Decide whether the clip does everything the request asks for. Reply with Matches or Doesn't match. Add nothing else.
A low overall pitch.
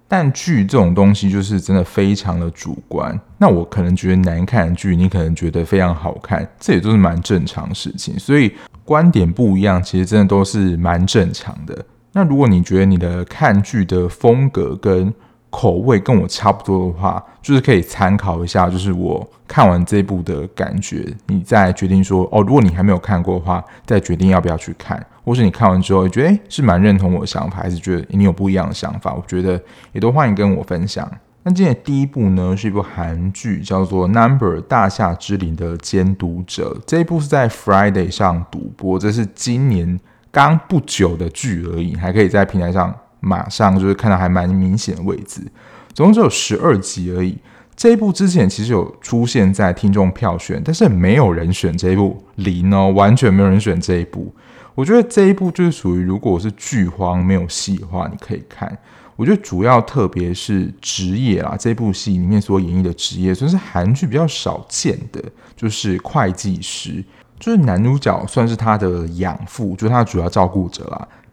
Matches